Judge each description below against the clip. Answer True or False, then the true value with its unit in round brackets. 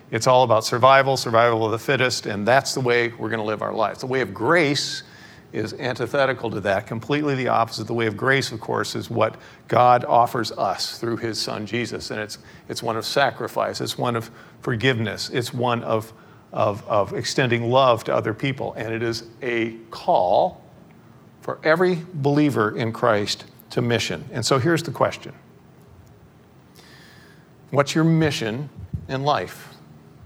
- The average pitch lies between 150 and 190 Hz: False (120 Hz)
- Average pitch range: True (3.0 semitones)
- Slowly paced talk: False (170 wpm)